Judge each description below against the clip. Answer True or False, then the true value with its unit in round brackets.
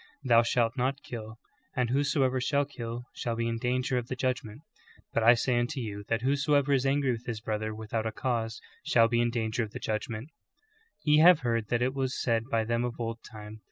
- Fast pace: True (225 wpm)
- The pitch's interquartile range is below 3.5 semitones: True (2.5 semitones)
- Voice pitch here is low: True (120 Hz)